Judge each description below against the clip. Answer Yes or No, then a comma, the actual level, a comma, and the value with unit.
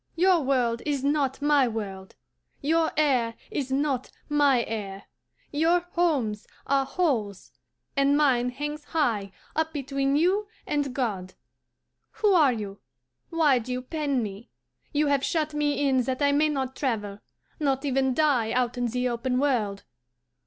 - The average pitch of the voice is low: No, very high, 270 Hz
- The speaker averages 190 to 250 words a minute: No, average, 150 wpm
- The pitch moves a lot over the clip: No, average, 3.8 semitones